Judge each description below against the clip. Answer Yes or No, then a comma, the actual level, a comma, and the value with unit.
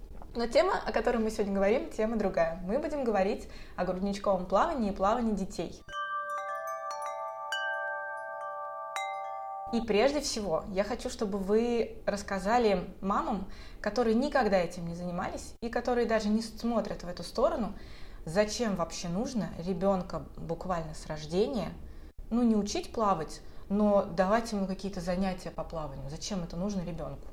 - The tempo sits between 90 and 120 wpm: No, average, 135 wpm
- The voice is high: Yes, high, 195 Hz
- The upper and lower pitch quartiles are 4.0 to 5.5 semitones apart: Yes, average, 4.5 semitones